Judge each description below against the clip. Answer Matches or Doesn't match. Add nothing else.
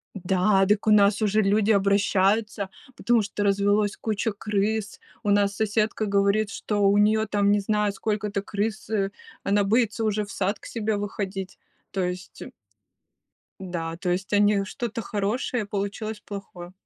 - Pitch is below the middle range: Doesn't match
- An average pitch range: Doesn't match